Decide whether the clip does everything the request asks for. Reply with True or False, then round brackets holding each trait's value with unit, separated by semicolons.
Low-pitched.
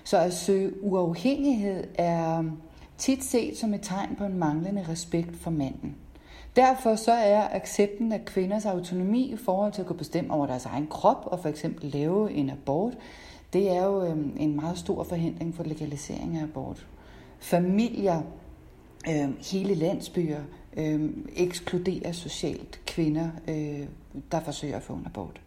False (170 Hz)